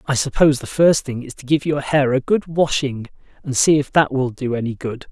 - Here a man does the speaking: Yes, male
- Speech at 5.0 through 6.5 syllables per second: Yes, 5.4 syllables/s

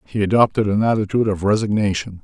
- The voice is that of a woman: No, male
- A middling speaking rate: Yes, average, 160 wpm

